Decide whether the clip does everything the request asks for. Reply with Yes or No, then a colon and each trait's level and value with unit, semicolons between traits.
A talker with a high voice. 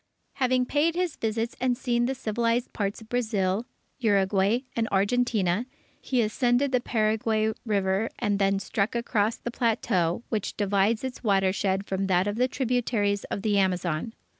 Yes: high, 220 Hz